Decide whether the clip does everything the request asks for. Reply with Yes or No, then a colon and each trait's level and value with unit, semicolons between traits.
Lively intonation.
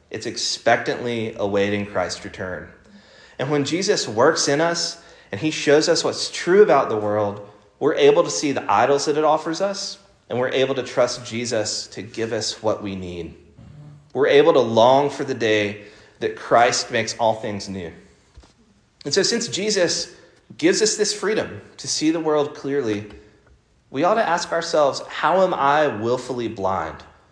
Yes: wide, 8.3 semitones